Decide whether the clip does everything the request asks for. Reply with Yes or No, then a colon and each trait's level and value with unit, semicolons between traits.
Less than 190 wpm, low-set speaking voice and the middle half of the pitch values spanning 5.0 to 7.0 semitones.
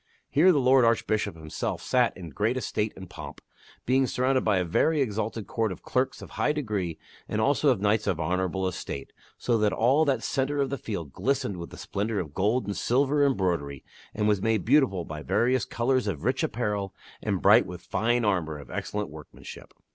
No: average, 200 wpm; low, 110 Hz; wide, 5.6 semitones